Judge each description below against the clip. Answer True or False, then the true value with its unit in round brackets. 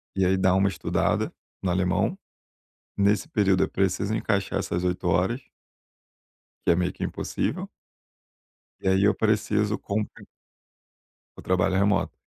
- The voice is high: False (95 Hz)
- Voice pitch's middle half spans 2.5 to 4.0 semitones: False (2.1 semitones)